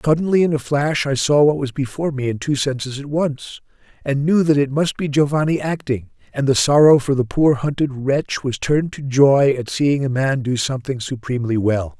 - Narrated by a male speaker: Yes, male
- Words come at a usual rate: No, fast, 215 wpm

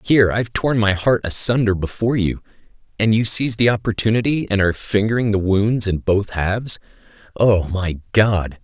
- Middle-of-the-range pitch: No, low, 105 Hz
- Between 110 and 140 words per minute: No, average, 165 wpm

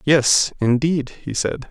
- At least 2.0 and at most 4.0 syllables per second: Yes, 3.3 syllables/s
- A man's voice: Yes, male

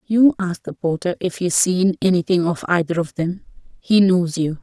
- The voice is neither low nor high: Yes, medium, 180 Hz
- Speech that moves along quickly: No, average, 180 wpm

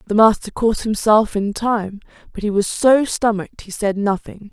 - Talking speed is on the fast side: No, average, 185 wpm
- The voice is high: Yes, high, 215 Hz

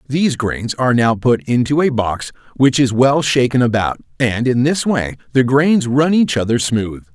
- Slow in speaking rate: No, average, 195 wpm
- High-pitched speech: No, low, 125 Hz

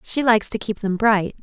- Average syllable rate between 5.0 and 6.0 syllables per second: Yes, 5.4 syllables/s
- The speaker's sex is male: No, female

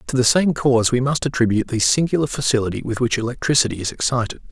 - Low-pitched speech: Yes, low, 125 Hz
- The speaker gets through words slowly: No, average, 200 wpm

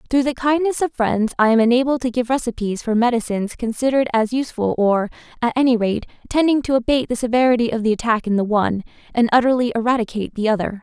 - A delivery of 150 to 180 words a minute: No, average, 200 wpm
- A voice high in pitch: Yes, high, 240 Hz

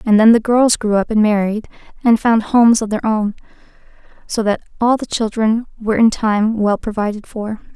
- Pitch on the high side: Yes, high, 220 Hz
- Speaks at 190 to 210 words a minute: Yes, average, 195 wpm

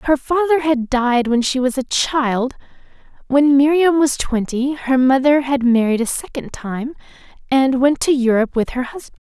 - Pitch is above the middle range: Yes, very high, 265 Hz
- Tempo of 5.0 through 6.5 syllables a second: No, 4.6 syllables/s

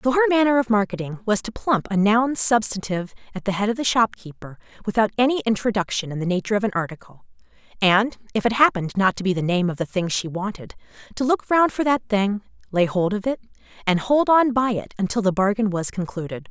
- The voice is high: Yes, high, 210 Hz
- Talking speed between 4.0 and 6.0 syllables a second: No, 6.2 syllables/s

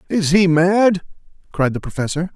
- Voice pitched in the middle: Yes, medium, 175 Hz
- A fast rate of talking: No, average, 155 wpm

